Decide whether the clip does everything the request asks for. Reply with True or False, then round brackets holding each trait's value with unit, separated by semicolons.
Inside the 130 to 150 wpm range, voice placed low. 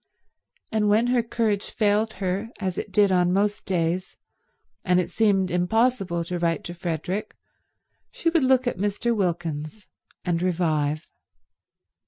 False (140 wpm; 190 Hz)